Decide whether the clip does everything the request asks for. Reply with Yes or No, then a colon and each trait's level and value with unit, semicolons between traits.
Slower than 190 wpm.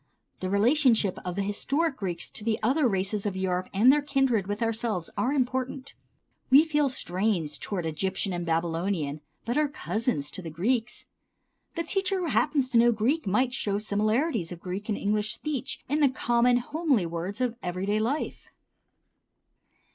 Yes: average, 170 wpm